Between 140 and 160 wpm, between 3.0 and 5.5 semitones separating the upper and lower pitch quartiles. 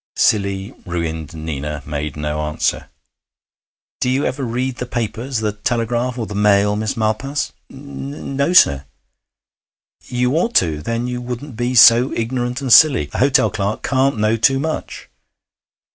Yes: average, 150 wpm; average, 4.7 semitones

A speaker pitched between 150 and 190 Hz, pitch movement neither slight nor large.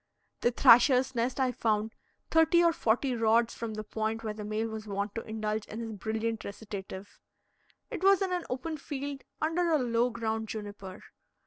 No: high, 230 Hz; average, 3.6 semitones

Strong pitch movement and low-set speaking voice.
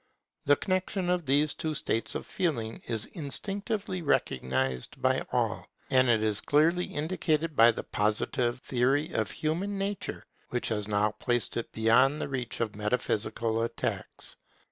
Yes: wide, 6.3 semitones; low, 130 Hz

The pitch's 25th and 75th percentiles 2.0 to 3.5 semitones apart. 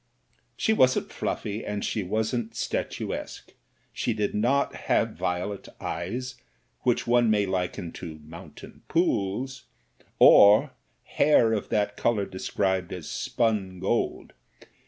No: average, 4.0 semitones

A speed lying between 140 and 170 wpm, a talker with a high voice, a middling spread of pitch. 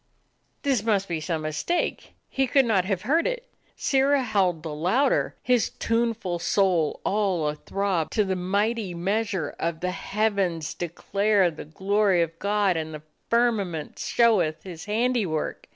Yes: average, 145 wpm; high, 195 Hz; average, 4.9 semitones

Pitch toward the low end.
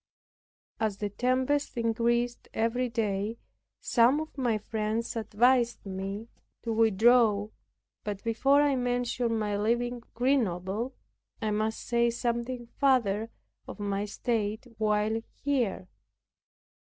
No: high, 230 Hz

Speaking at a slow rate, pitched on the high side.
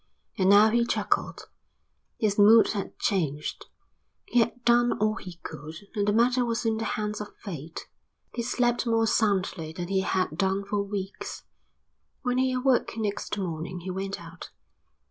No: average, 165 wpm; high, 205 Hz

